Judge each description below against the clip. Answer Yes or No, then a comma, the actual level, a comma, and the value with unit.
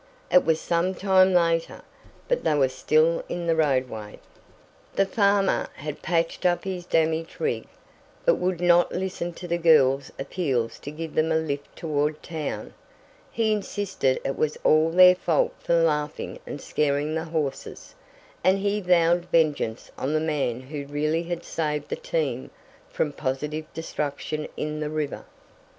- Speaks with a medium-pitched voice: Yes, medium, 160 Hz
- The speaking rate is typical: Yes, average, 155 wpm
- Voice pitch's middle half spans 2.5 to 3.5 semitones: Yes, average, 3.0 semitones